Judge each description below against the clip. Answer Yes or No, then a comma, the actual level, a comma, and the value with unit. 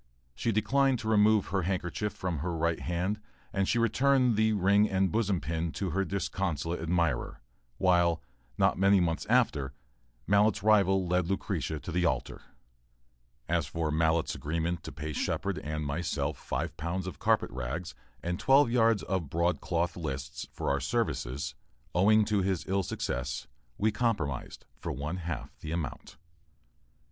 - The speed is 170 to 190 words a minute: No, average, 155 wpm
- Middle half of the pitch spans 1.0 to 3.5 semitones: No, average, 4.3 semitones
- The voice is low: Yes, very low, 90 Hz